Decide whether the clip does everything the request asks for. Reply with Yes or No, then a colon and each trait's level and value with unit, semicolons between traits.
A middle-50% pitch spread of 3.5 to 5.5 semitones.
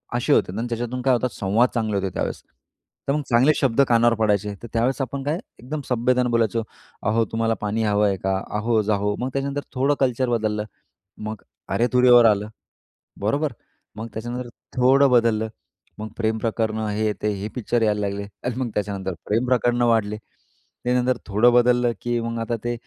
No: narrow, 2.6 semitones